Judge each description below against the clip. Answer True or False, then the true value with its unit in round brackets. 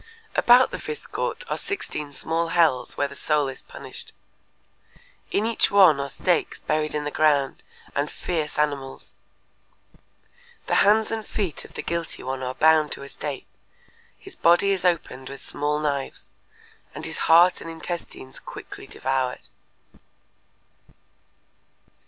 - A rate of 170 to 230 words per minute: False (140 wpm)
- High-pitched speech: False (155 Hz)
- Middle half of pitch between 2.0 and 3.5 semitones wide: False (4.0 semitones)